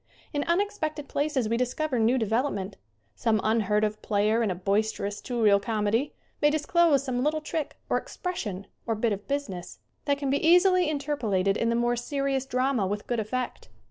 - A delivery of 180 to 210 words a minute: Yes, average, 185 wpm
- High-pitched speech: Yes, high, 245 Hz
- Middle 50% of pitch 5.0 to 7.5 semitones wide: Yes, average, 5.3 semitones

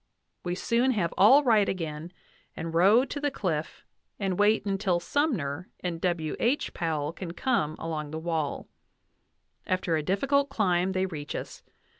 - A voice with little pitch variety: No, average, 4.9 semitones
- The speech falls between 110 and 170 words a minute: Yes, average, 155 wpm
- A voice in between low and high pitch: Yes, medium, 180 Hz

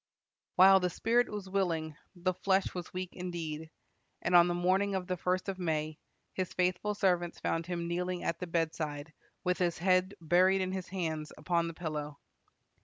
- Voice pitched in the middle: Yes, medium, 180 Hz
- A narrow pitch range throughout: Yes, narrow, 2.1 semitones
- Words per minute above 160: Yes, average, 180 wpm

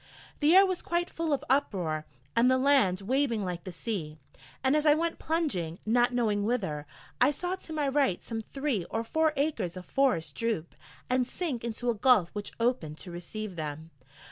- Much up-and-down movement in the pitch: Yes, wide, 7.8 semitones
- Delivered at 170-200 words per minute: Yes, average, 190 wpm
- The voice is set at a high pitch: Yes, high, 235 Hz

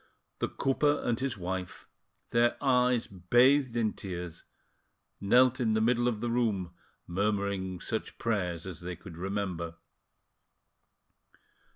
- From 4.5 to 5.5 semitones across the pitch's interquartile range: Yes, average, 4.9 semitones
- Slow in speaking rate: Yes, slow, 125 wpm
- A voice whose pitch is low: Yes, low, 105 Hz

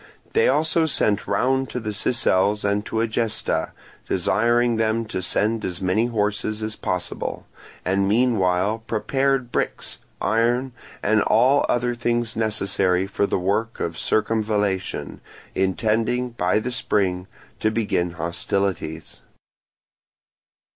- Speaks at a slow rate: Yes, slow, 120 wpm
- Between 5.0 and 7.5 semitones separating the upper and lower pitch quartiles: No, average, 3.4 semitones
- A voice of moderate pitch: No, low, 110 Hz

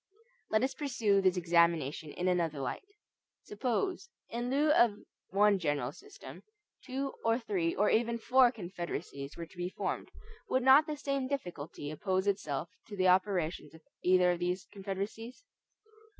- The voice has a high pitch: Yes, high, 195 Hz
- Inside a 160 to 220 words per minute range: No, average, 150 wpm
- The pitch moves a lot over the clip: Yes, wide, 5.9 semitones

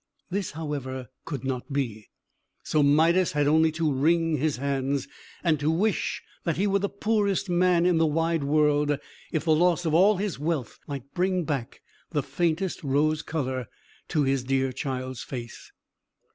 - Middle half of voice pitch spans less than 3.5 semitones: No, average, 3.8 semitones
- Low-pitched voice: No, medium, 155 Hz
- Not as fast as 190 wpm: Yes, average, 165 wpm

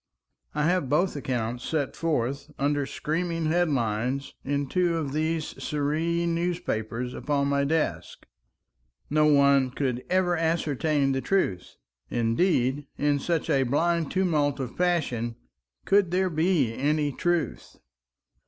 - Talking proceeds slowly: Yes, slow, 125 wpm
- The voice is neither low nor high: Yes, medium, 150 Hz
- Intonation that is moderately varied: Yes, average, 3.8 semitones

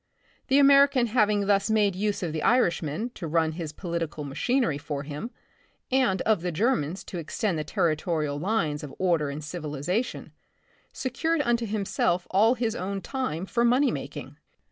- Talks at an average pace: Yes, average, 165 wpm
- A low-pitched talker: No, high, 190 Hz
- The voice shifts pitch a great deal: Yes, wide, 7.0 semitones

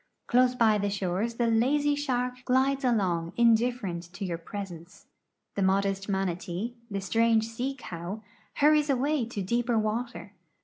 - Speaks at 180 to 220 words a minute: No, average, 140 wpm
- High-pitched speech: Yes, high, 225 Hz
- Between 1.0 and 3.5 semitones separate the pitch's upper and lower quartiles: No, average, 4.3 semitones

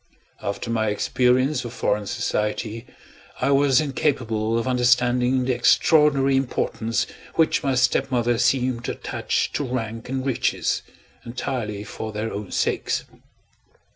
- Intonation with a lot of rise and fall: No, average, 2.8 semitones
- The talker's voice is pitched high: No, low, 125 Hz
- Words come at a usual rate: No, slow, 125 wpm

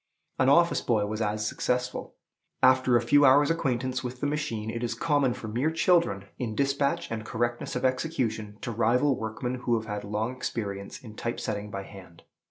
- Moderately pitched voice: No, low, 120 Hz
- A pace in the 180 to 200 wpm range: Yes, average, 185 wpm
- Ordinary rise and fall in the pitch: Yes, average, 3.6 semitones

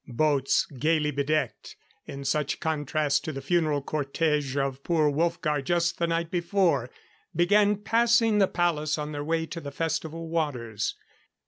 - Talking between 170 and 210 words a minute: No, average, 145 wpm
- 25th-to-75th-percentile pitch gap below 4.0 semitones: Yes, average, 3.0 semitones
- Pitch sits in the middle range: Yes, medium, 155 Hz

